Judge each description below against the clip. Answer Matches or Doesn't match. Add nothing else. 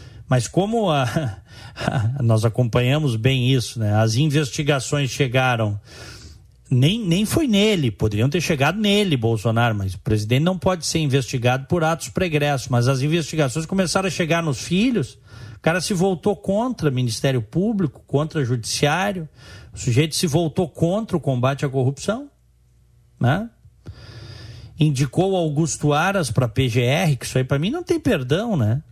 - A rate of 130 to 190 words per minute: Matches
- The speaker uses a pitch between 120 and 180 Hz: Matches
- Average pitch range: Doesn't match